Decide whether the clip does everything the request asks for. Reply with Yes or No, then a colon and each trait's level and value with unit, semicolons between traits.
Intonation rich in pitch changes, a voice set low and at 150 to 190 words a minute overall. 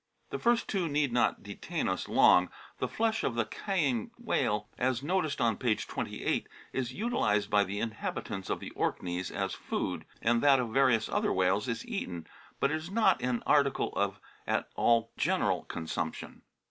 Yes: wide, 6.3 semitones; low, 120 Hz; average, 170 wpm